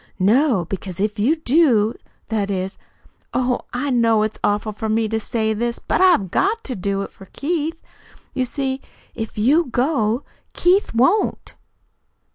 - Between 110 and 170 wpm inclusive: Yes, average, 155 wpm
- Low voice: No, high, 230 Hz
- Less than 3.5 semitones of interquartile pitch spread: No, average, 5.0 semitones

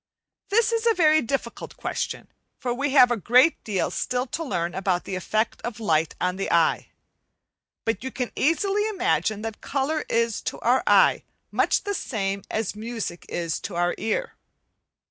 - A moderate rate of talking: Yes, average, 170 wpm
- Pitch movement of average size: No, wide, 7.5 semitones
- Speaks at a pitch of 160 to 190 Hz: No, high, 235 Hz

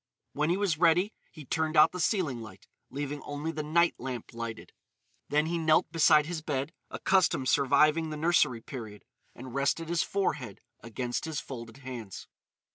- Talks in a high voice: No, medium, 150 Hz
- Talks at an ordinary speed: Yes, average, 160 wpm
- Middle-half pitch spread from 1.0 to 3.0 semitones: No, average, 4.1 semitones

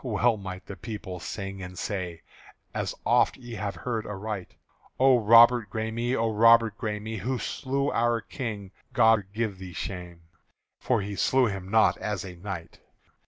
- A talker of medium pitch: No, low, 105 Hz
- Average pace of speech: Yes, average, 160 wpm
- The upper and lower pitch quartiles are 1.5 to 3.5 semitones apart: Yes, average, 3.2 semitones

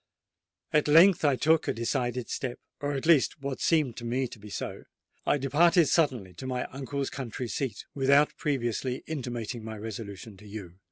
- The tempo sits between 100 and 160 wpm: No, average, 170 wpm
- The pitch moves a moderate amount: Yes, average, 3.9 semitones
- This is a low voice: Yes, low, 130 Hz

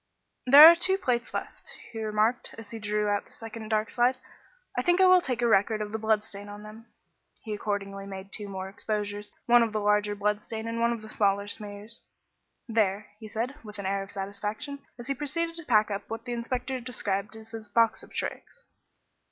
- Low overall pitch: No, high, 220 Hz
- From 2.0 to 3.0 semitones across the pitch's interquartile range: Yes, narrow, 2.6 semitones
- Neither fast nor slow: No, fast, 215 wpm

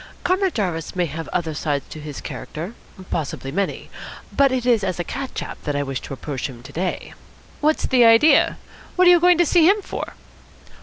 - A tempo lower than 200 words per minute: No, fast, 205 wpm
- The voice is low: No, medium, 185 Hz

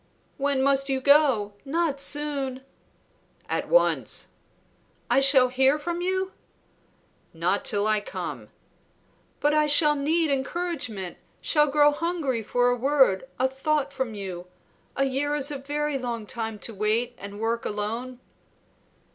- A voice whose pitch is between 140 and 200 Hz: No, very high, 270 Hz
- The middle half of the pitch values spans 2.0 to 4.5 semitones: Yes, average, 4.1 semitones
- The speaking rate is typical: No, slow, 130 wpm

